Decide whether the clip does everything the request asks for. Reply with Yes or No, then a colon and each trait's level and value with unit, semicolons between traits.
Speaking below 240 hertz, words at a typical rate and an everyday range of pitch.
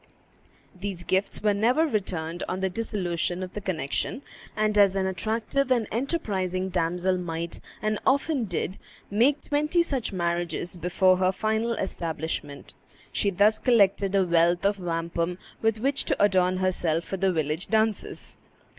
Yes: high, 190 Hz; average, 145 wpm; average, 3.7 semitones